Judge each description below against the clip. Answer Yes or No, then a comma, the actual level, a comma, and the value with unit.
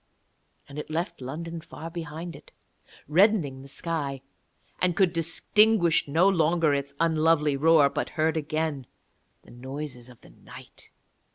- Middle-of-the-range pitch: Yes, medium, 160 Hz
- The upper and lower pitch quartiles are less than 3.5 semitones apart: Yes, average, 3.0 semitones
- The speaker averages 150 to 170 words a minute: No, average, 140 wpm